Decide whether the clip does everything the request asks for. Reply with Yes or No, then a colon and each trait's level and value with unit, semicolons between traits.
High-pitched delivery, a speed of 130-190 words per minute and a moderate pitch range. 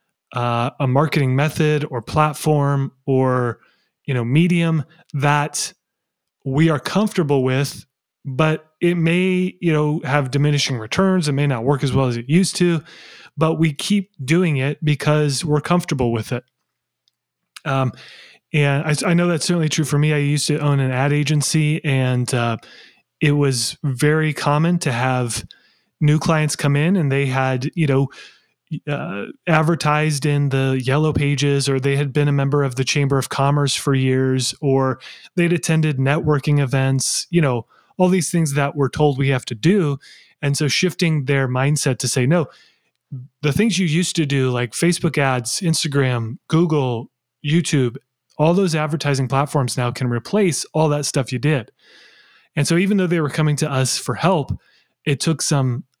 No: medium, 145 Hz; average, 170 wpm; average, 3.1 semitones